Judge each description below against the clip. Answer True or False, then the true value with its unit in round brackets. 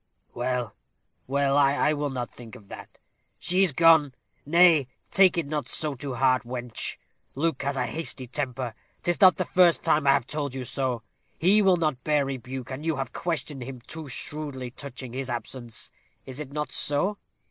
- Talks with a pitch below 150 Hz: True (140 Hz)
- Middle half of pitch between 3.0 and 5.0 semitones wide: True (3.3 semitones)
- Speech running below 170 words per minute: False (180 wpm)